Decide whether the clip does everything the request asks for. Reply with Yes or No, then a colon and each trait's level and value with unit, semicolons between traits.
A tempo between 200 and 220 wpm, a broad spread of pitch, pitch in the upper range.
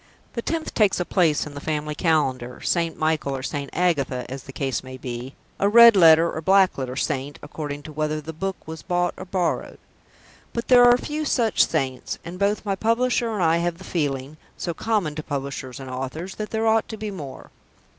No: fast, 205 wpm; wide, 6.0 semitones; medium, 160 Hz